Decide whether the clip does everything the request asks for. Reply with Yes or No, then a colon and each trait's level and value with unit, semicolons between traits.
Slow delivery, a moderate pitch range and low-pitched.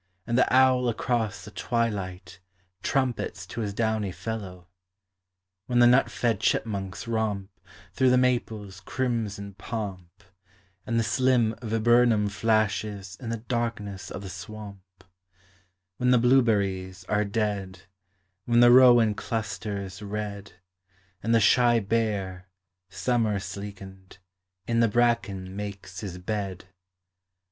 Yes: slow, 120 wpm; average, 3.2 semitones; low, 105 Hz